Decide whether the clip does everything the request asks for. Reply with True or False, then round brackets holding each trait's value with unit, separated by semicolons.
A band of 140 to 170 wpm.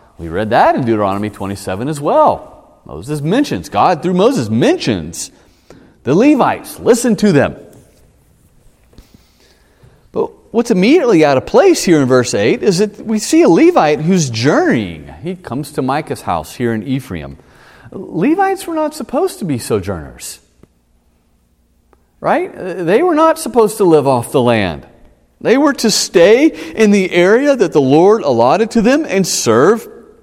True (155 wpm)